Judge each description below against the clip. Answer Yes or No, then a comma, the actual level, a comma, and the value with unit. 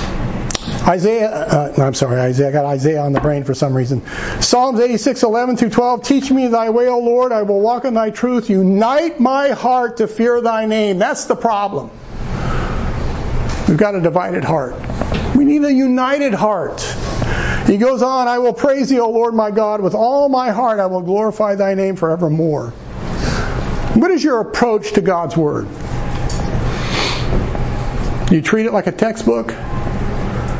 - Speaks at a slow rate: No, average, 165 wpm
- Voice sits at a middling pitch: No, high, 220 Hz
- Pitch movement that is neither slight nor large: No, wide, 5.9 semitones